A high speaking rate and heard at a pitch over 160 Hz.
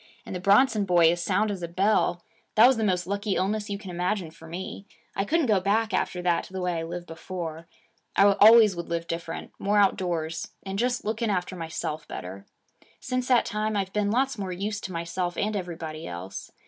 Yes: fast, 210 wpm; high, 190 Hz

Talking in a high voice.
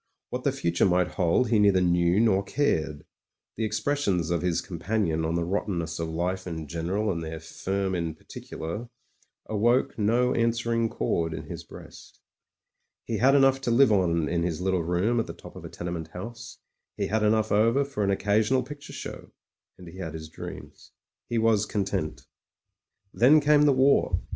No: low, 100 Hz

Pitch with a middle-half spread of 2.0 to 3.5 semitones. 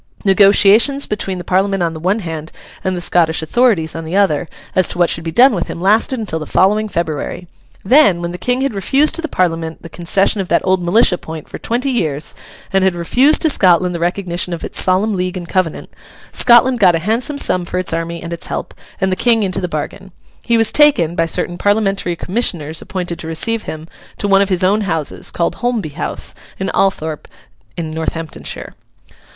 No: average, 3.9 semitones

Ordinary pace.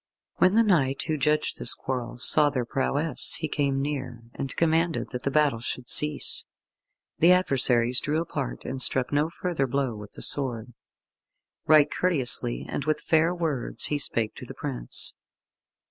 Yes: average, 160 wpm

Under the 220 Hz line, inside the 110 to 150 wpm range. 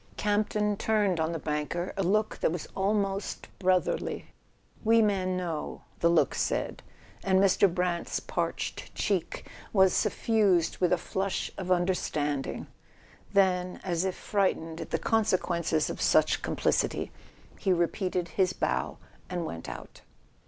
Yes: medium, 185 Hz; average, 140 wpm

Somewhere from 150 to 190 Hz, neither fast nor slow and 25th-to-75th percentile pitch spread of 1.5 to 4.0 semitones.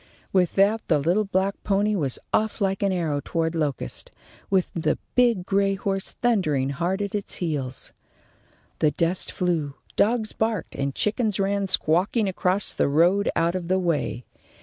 Yes: medium, 185 Hz; average, 160 wpm; average, 3.7 semitones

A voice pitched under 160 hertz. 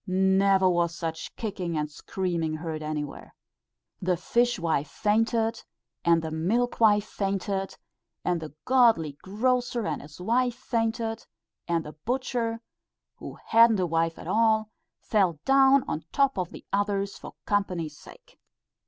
No: high, 195 Hz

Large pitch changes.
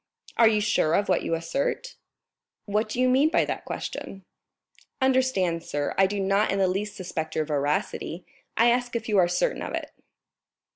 Yes: wide, 5.7 semitones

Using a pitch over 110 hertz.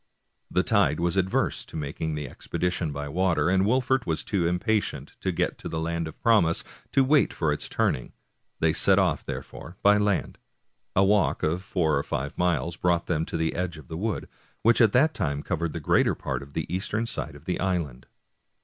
No: very low, 85 Hz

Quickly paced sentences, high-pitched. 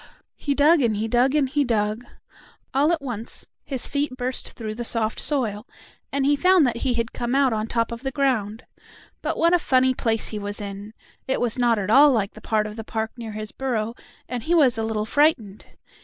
Yes: fast, 220 wpm; high, 240 Hz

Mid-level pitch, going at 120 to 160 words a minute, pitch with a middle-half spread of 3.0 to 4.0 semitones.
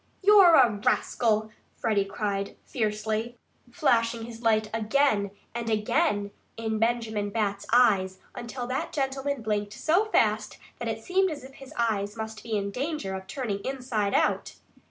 No: high, 225 Hz; average, 150 wpm; average, 3.6 semitones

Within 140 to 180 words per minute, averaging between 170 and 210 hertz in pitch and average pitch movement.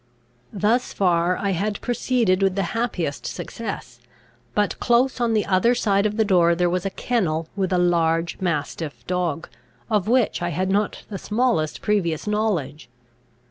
Yes: average, 160 wpm; high, 190 Hz; average, 3.9 semitones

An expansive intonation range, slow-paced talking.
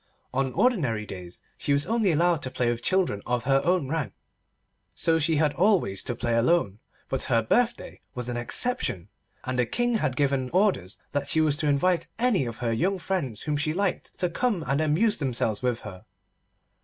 No: wide, 7.0 semitones; average, 190 wpm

